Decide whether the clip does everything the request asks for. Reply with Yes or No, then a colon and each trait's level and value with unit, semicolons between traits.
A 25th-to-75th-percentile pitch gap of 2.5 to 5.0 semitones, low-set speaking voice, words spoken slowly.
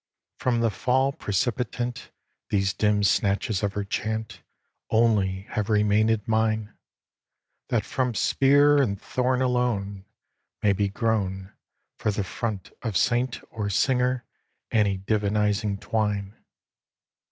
Yes: average, 3.2 semitones; low, 110 Hz; slow, 115 wpm